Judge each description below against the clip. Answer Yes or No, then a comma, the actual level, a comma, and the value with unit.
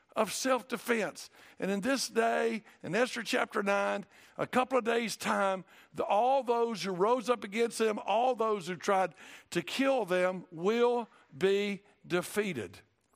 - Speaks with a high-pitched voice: Yes, high, 220 Hz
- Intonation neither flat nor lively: Yes, average, 3.6 semitones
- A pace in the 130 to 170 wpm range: Yes, average, 155 wpm